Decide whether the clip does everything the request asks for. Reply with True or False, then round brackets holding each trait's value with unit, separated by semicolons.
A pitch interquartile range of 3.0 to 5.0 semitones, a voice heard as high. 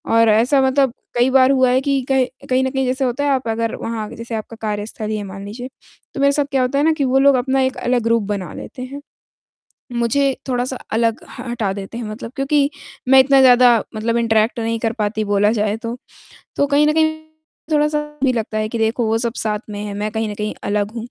True (3.5 semitones; 240 Hz)